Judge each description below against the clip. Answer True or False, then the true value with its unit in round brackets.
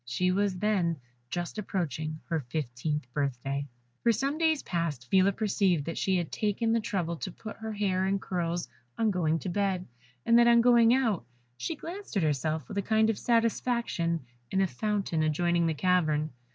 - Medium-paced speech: True (180 wpm)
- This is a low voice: False (185 Hz)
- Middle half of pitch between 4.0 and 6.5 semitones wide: True (5.4 semitones)